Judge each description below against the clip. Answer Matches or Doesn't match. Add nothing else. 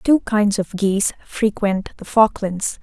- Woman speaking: Matches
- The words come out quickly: Doesn't match